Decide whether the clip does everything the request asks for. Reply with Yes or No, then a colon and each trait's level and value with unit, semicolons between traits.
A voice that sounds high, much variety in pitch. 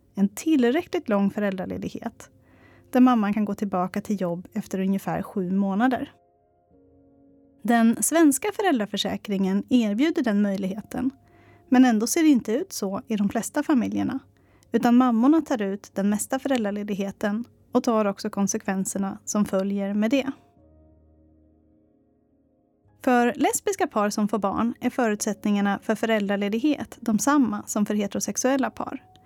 No: high, 215 Hz; average, 4.2 semitones